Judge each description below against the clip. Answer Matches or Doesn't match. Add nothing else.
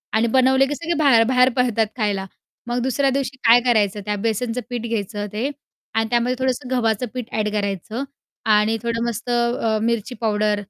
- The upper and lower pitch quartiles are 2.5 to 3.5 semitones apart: Matches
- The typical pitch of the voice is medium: Doesn't match